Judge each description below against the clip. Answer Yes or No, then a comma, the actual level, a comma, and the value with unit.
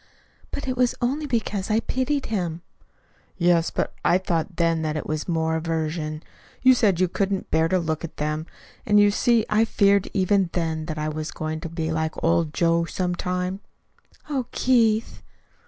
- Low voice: No, medium, 175 Hz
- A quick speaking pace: No, average, 180 wpm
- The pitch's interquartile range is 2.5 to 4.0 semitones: No, average, 4.6 semitones